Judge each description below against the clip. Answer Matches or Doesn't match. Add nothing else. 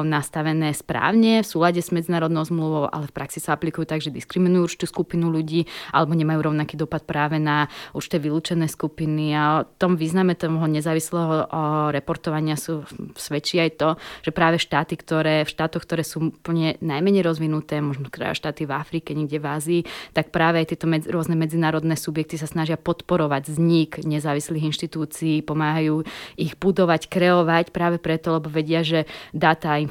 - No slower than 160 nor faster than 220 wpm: Matches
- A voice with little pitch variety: Matches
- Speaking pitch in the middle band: Matches